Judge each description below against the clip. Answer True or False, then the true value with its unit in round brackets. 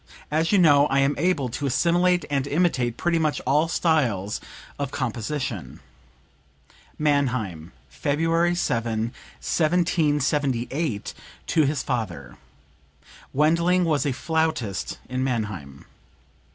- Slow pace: True (105 wpm)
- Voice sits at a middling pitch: True (145 Hz)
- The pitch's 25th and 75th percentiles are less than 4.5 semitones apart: False (5.1 semitones)